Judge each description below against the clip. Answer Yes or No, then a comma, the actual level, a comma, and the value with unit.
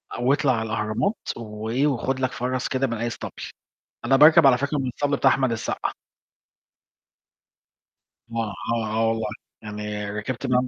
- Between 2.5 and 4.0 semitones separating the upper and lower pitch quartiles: Yes, average, 3.3 semitones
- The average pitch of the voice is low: Yes, low, 125 Hz